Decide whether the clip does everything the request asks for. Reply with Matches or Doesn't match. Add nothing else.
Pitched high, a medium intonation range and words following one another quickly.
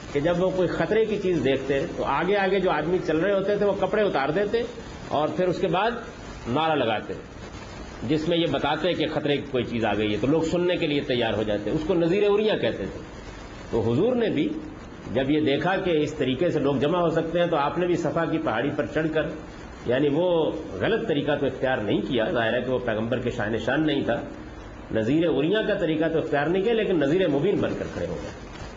Doesn't match